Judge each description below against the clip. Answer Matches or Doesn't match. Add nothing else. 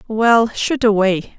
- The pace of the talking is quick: Doesn't match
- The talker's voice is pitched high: Matches